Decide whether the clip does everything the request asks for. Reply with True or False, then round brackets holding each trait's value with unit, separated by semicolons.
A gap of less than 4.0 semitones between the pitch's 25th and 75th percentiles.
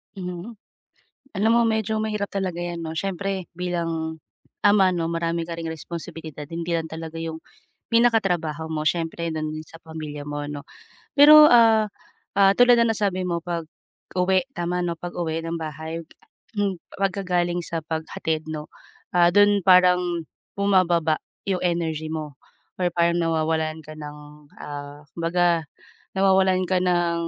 True (2.8 semitones)